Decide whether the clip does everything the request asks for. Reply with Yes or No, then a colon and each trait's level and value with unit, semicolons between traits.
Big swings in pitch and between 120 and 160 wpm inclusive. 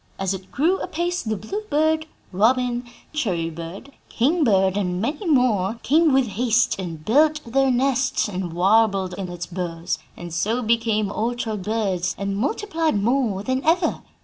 Yes: wide, 6.2 semitones; average, 150 wpm